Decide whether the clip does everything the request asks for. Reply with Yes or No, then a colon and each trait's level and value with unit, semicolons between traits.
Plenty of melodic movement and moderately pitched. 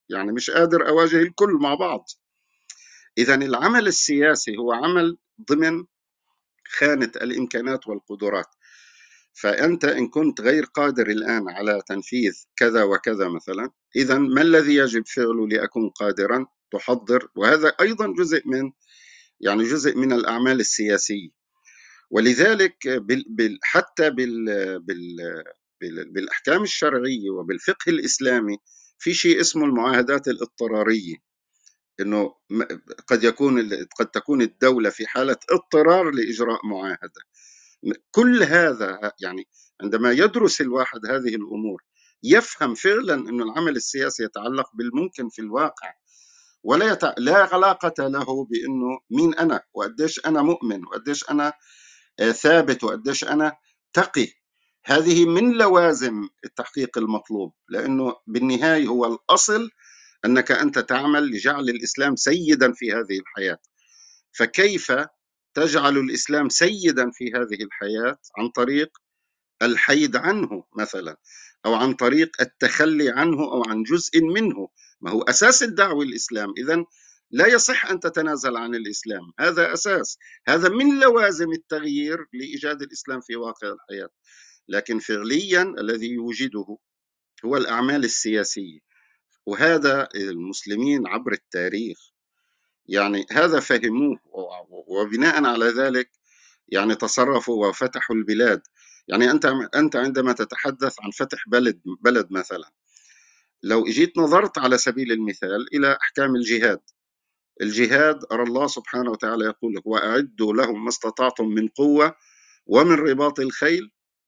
No: wide, 5.8 semitones; low, 130 Hz